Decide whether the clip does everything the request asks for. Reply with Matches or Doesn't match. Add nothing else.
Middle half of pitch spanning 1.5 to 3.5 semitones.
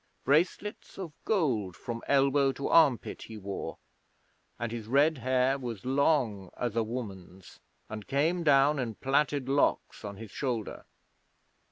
Doesn't match